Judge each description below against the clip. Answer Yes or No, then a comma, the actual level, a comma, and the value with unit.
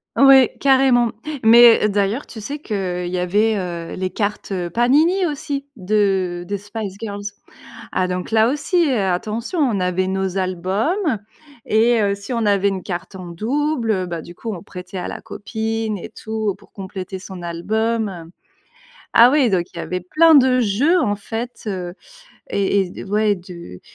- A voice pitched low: No, high, 205 Hz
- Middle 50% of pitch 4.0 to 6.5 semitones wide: Yes, average, 4.3 semitones